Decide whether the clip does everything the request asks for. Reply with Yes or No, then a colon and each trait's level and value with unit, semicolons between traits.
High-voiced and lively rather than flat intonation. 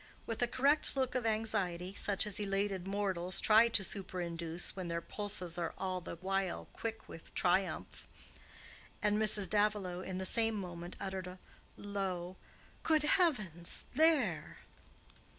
No: high, 195 Hz; average, 3.3 semitones